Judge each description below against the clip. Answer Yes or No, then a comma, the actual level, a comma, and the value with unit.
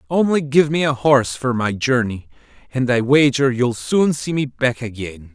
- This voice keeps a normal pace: Yes, average, 190 wpm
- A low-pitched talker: Yes, low, 130 Hz